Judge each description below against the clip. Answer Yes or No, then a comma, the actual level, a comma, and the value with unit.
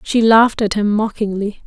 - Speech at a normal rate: Yes, average, 180 wpm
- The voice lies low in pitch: No, high, 215 Hz